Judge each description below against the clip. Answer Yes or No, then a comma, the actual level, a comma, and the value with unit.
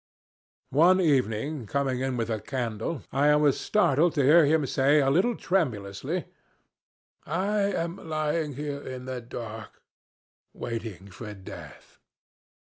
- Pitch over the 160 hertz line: No, medium, 140 Hz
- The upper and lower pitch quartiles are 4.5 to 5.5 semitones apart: Yes, average, 5.1 semitones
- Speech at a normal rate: No, slow, 125 wpm